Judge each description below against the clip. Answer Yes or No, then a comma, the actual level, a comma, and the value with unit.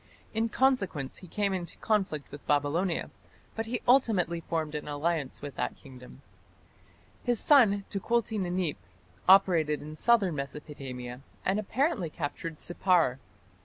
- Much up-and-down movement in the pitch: Yes, wide, 6.0 semitones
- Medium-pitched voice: Yes, medium, 175 Hz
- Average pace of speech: No, slow, 130 wpm